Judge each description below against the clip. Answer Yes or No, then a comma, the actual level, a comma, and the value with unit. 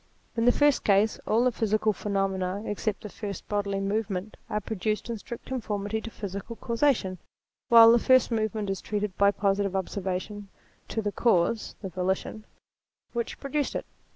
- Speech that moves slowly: No, average, 175 wpm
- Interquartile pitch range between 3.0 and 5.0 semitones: No, narrow, 2.5 semitones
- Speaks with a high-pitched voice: Yes, high, 210 Hz